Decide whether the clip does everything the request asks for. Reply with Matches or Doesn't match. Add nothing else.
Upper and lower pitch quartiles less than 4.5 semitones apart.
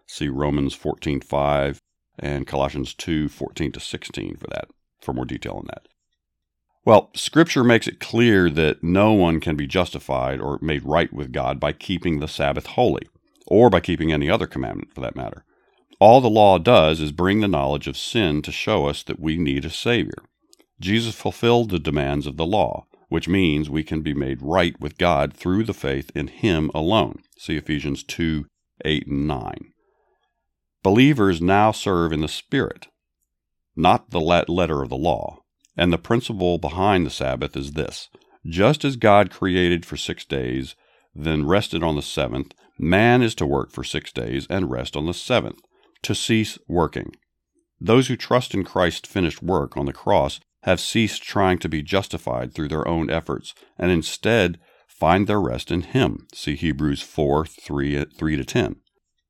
Doesn't match